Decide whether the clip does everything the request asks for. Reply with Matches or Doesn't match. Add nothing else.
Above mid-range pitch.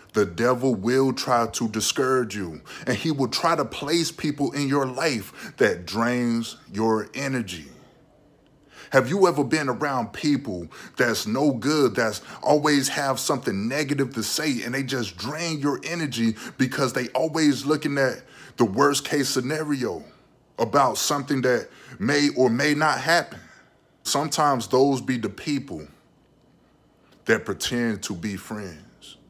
Doesn't match